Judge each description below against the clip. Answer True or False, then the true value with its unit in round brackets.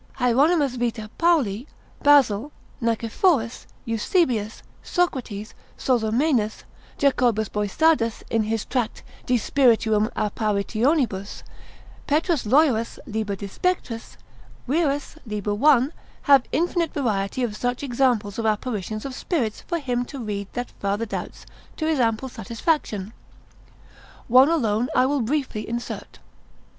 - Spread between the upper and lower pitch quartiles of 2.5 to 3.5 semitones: False (4.7 semitones)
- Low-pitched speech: False (240 Hz)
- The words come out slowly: True (120 wpm)